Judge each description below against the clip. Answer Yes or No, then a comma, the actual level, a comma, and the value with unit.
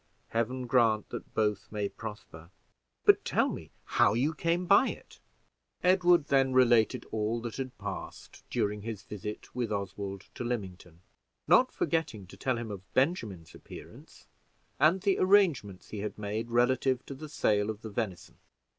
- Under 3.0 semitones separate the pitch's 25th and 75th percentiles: No, average, 4.5 semitones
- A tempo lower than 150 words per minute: No, average, 155 wpm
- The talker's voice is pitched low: Yes, low, 115 Hz